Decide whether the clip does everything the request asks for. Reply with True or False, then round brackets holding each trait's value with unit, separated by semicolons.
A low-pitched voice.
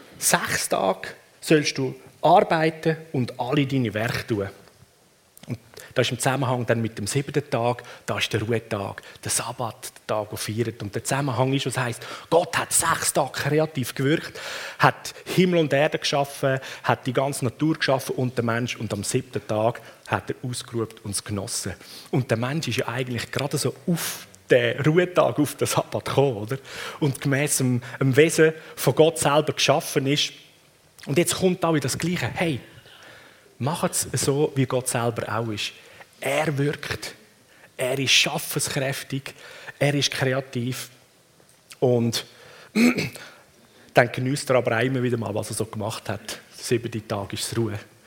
True (130 Hz)